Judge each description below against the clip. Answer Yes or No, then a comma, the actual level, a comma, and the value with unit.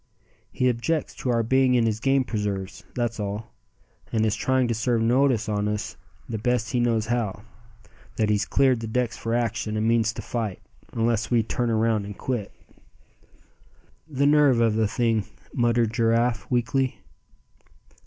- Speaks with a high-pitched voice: No, low, 115 Hz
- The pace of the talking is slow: No, average, 165 wpm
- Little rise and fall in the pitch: Yes, narrow, 2.1 semitones